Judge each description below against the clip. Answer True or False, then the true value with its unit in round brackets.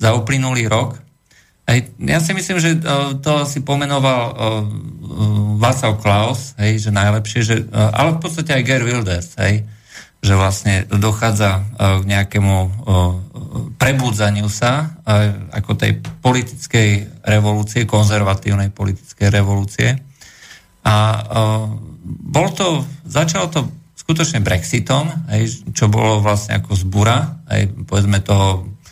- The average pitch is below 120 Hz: True (110 Hz)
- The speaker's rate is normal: False (100 wpm)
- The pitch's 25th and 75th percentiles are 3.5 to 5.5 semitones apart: True (4.6 semitones)